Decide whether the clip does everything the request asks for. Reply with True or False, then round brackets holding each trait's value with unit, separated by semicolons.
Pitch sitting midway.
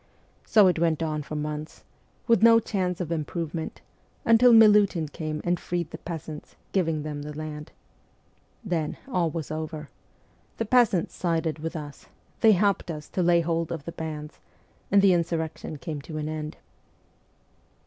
True (165 Hz)